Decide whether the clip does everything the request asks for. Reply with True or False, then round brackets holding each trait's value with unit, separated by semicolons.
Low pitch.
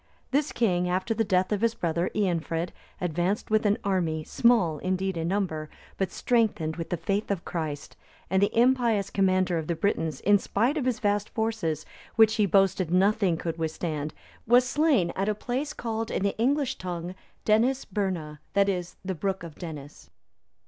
False (190 Hz)